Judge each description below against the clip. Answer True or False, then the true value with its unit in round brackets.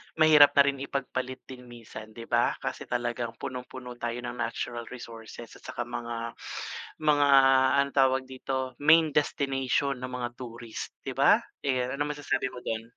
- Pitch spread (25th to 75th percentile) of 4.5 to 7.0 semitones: False (2.5 semitones)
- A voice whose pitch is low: True (125 Hz)